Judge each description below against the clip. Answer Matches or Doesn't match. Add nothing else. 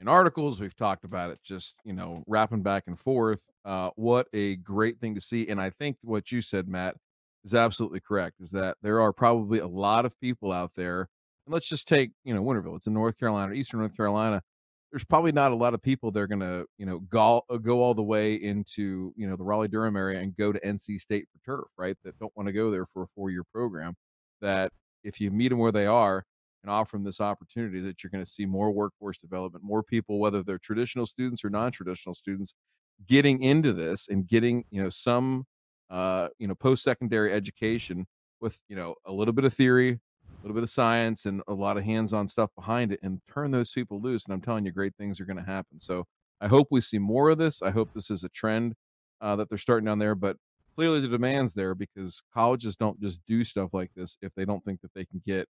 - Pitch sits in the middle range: Doesn't match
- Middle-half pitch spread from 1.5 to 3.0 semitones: Doesn't match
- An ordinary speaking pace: Doesn't match